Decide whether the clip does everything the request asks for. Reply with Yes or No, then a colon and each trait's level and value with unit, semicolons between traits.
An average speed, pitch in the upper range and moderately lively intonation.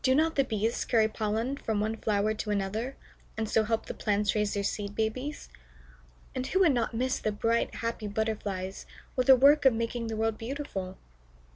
Yes: average, 190 wpm; high, 225 Hz; average, 3.2 semitones